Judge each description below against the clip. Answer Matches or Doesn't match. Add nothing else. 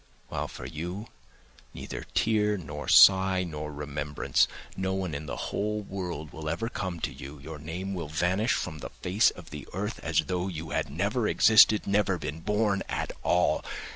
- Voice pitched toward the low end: Matches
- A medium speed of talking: Matches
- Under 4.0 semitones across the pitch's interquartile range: Doesn't match